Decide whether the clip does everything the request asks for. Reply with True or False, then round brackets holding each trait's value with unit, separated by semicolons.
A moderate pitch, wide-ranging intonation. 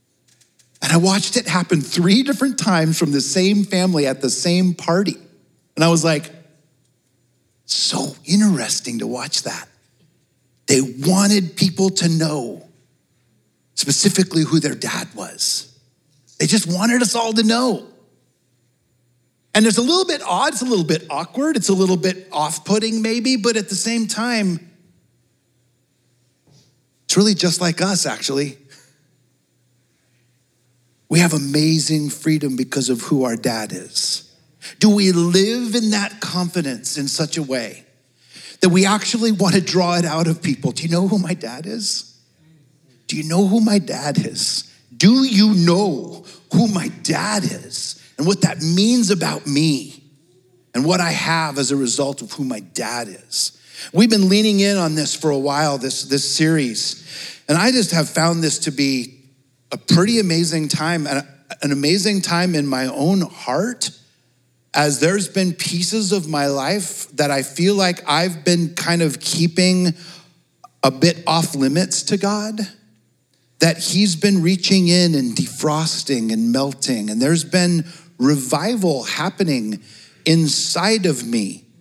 True (165 Hz; 5.7 semitones)